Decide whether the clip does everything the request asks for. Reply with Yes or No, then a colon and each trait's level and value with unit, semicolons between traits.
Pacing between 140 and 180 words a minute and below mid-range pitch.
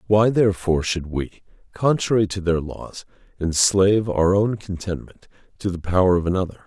Yes: average, 155 wpm; very low, 95 Hz